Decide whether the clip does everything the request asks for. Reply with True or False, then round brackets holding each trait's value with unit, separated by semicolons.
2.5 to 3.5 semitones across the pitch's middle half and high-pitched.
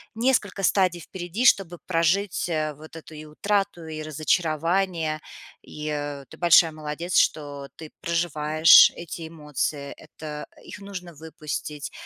False (2.8 semitones; 165 Hz)